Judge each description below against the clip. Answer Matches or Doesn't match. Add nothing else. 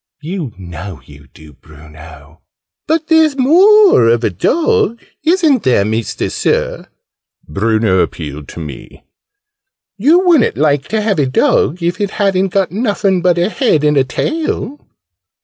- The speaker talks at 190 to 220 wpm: Doesn't match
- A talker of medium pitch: Matches